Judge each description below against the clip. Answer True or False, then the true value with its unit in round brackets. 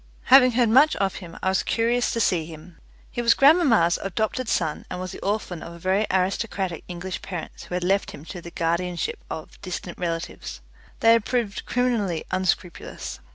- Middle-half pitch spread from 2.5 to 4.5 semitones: False (4.9 semitones)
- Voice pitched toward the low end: False (190 Hz)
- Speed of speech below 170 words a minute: False (180 wpm)